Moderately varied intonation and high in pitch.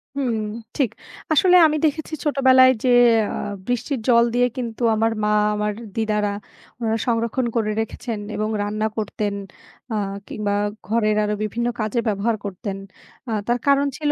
Yes: average, 3.3 semitones; high, 230 Hz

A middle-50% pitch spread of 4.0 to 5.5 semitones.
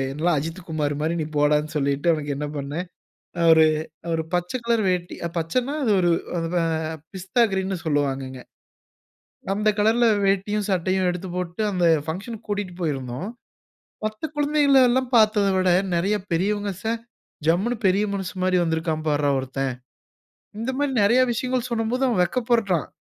Yes: average, 5.2 semitones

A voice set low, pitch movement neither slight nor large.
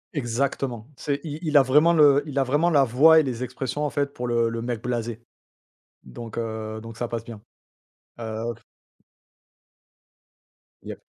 Yes: low, 125 Hz; average, 3.7 semitones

